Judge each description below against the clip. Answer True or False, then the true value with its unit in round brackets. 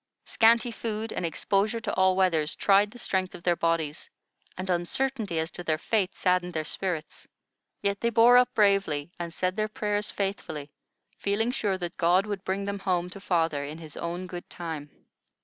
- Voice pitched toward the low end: False (185 Hz)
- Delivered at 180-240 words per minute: True (185 wpm)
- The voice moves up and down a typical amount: True (3.5 semitones)